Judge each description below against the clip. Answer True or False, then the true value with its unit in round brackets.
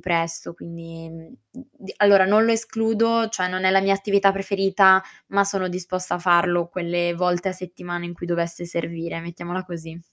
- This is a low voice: False (180 Hz)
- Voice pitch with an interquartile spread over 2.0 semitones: True (2.4 semitones)